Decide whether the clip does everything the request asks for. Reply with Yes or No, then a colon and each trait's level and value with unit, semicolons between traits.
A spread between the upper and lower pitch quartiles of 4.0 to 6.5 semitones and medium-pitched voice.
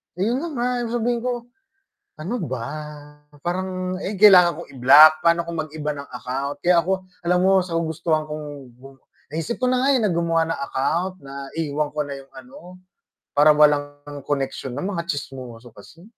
Yes: average, 4.4 semitones; medium, 160 Hz